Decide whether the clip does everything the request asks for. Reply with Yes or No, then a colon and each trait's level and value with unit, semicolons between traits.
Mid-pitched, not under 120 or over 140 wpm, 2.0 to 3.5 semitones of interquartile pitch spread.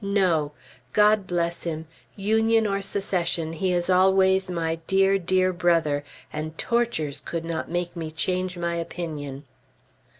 Yes: medium, 175 Hz; slow, 135 wpm; average, 2.9 semitones